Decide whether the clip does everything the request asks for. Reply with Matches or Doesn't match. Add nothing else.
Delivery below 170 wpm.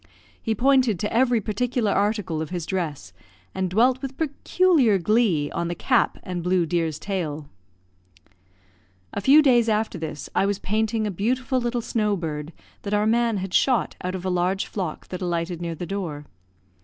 Doesn't match